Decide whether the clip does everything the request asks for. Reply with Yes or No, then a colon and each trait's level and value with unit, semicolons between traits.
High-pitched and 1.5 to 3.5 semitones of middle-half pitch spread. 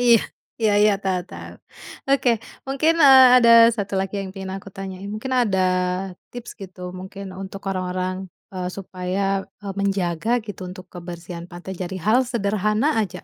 Yes: high, 195 Hz; average, 2.7 semitones